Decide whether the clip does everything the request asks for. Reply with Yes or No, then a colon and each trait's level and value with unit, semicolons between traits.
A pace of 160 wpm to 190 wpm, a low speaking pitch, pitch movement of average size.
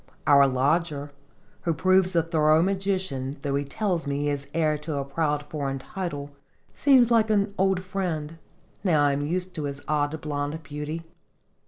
No: average, 170 wpm; medium, 155 Hz; average, 4.3 semitones